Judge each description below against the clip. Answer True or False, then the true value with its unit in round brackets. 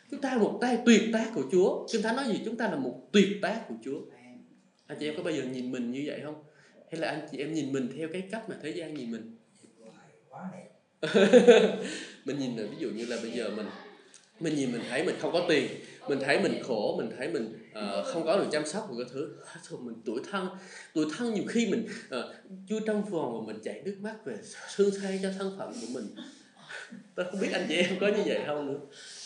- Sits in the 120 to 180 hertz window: False (200 Hz)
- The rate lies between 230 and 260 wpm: True (240 wpm)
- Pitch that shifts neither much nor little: False (6.3 semitones)